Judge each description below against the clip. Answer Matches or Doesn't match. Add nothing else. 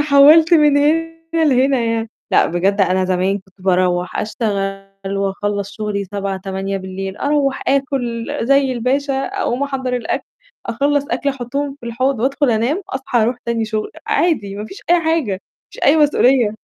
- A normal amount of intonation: Doesn't match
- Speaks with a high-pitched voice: Matches